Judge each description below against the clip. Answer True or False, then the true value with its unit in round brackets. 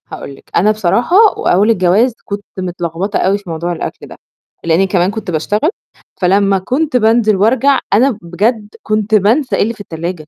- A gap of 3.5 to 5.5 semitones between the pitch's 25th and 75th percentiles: True (4.1 semitones)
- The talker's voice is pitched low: False (205 Hz)